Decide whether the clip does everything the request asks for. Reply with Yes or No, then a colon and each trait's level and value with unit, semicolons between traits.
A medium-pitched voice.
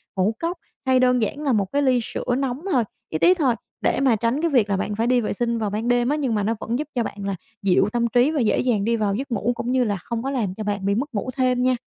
No: high, 240 Hz